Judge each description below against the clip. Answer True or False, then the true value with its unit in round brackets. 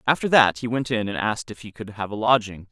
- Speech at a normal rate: False (290 wpm)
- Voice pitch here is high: False (110 Hz)